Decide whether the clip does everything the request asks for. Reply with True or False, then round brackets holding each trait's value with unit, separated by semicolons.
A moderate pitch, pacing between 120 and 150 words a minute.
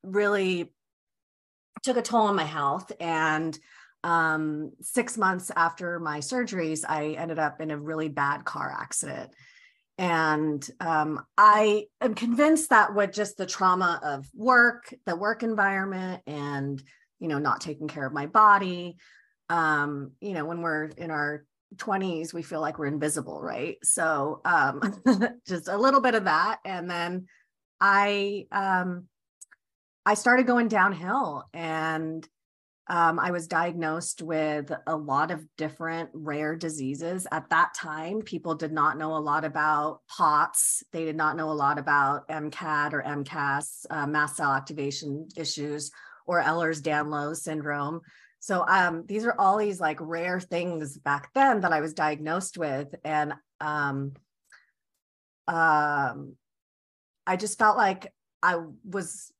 True (165 Hz; 145 wpm)